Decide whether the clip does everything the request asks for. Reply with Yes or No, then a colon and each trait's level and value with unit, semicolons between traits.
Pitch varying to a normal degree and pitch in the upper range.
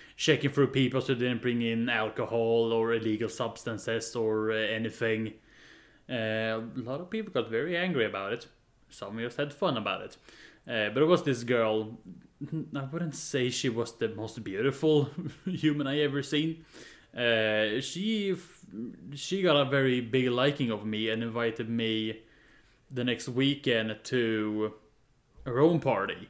No: average, 4.3 semitones; low, 125 Hz